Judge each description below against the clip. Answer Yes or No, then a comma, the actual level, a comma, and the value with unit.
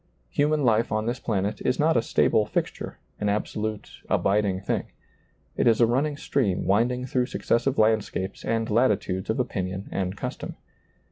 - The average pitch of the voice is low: Yes, low, 110 Hz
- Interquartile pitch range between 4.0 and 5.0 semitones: No, average, 3.5 semitones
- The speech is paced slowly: No, average, 165 wpm